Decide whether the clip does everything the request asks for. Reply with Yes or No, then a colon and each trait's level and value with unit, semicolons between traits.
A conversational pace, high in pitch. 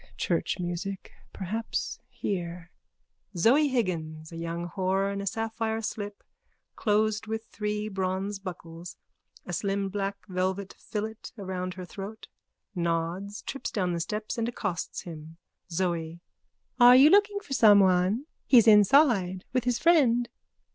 No: slow, 130 wpm; high, 200 Hz